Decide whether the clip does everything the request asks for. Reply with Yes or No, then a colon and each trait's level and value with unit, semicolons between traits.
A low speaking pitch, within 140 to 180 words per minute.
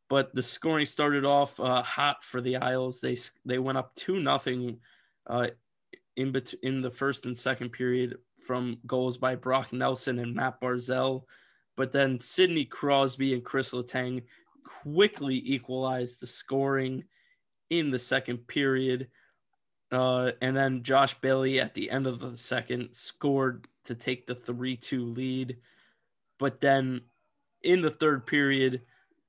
Yes: low, 130 Hz; average, 145 wpm